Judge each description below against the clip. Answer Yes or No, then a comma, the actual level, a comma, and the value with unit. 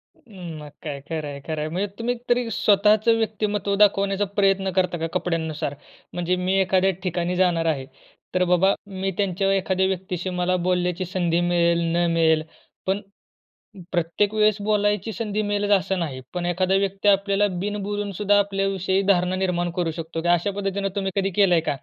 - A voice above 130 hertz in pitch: Yes, high, 190 Hz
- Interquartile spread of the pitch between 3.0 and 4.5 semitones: No, narrow, 2.6 semitones